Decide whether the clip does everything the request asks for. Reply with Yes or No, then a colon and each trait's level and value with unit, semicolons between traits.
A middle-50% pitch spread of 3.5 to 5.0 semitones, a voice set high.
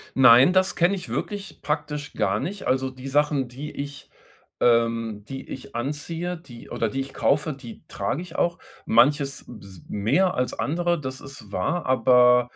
No: average, 4.0 semitones; low, 135 Hz